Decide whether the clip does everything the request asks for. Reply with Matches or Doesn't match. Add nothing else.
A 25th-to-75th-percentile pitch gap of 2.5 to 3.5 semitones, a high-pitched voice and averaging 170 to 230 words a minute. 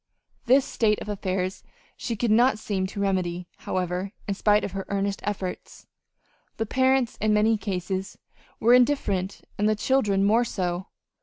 Doesn't match